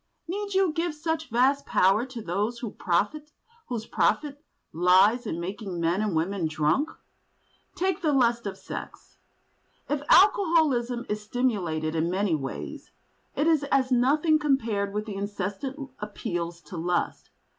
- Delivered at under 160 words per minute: Yes, slow, 135 wpm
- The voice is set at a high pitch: Yes, high, 230 Hz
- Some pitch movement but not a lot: No, wide, 7.4 semitones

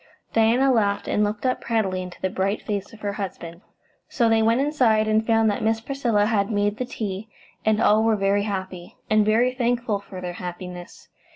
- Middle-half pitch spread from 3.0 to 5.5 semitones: No, narrow, 2.4 semitones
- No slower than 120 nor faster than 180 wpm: No, average, 195 wpm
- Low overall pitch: No, high, 215 Hz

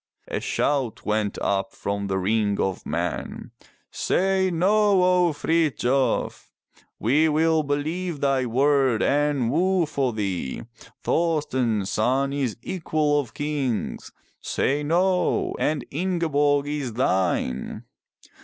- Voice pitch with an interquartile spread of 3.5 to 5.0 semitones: No, wide, 5.6 semitones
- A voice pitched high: No, medium, 145 Hz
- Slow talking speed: Yes, slow, 115 wpm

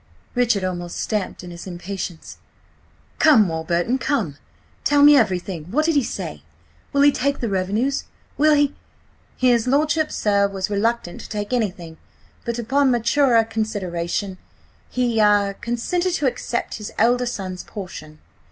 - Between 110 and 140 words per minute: Yes, slow, 135 wpm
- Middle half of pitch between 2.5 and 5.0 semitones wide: No, wide, 5.5 semitones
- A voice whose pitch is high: Yes, high, 220 Hz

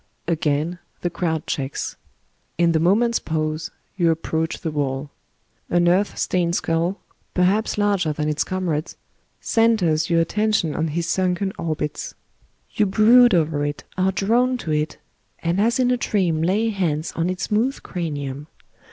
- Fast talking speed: No, average, 150 wpm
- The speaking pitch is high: No, medium, 170 Hz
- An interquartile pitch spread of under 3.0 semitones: No, average, 4.3 semitones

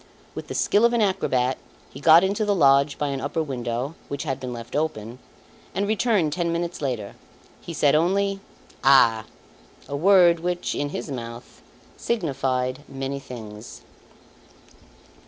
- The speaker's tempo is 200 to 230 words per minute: No, average, 150 wpm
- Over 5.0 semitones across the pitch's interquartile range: Yes, wide, 5.4 semitones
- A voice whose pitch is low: No, medium, 145 Hz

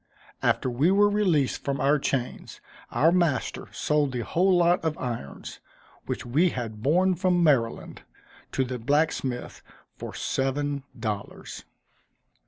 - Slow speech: Yes, slow, 130 wpm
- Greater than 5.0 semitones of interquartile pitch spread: Yes, wide, 5.5 semitones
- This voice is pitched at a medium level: Yes, medium, 145 Hz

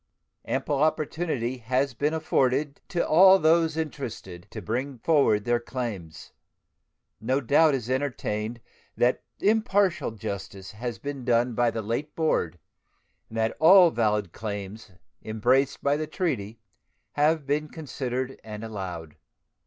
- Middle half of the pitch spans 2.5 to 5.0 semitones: No, wide, 5.4 semitones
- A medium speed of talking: No, slow, 130 wpm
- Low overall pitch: Yes, low, 125 Hz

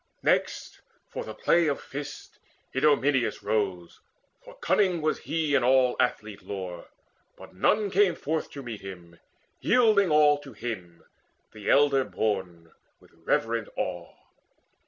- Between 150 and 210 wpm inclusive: No, slow, 135 wpm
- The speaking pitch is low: Yes, low, 125 Hz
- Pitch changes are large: Yes, wide, 7.7 semitones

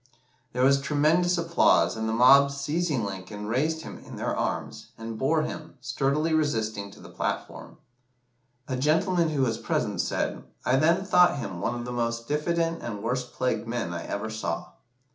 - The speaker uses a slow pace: No, average, 175 wpm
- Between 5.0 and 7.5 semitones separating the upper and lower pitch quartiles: Yes, wide, 5.5 semitones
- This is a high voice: No, low, 130 Hz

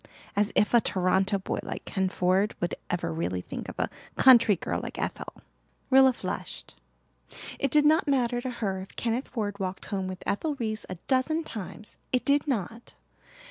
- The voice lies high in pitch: Yes, high, 215 Hz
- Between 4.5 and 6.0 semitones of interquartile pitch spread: Yes, wide, 5.4 semitones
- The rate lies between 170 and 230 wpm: Yes, average, 180 wpm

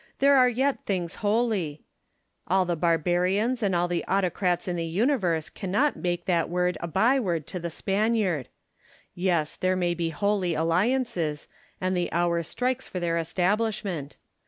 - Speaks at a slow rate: No, average, 155 wpm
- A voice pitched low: No, medium, 180 Hz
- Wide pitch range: No, average, 3.7 semitones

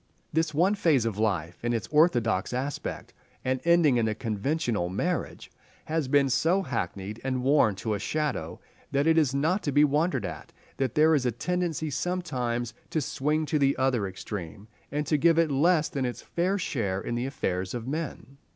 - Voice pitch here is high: No, low, 135 Hz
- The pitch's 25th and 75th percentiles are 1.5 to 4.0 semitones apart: No, wide, 5.6 semitones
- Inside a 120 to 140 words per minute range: No, average, 190 wpm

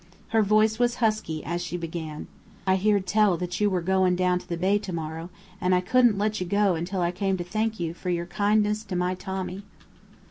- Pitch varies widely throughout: No, average, 3.0 semitones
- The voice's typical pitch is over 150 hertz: Yes, medium, 185 Hz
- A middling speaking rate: No, fast, 215 wpm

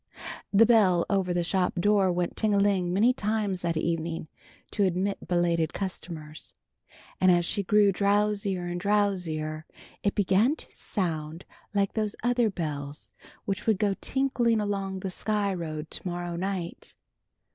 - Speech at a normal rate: Yes, average, 150 wpm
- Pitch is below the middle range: No, high, 190 Hz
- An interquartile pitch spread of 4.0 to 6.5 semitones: No, average, 3.0 semitones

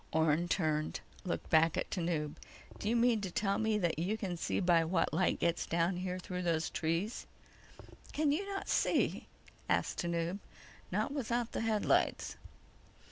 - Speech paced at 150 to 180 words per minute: Yes, average, 160 wpm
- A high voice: No, medium, 180 Hz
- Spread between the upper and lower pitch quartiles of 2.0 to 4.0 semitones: No, average, 4.6 semitones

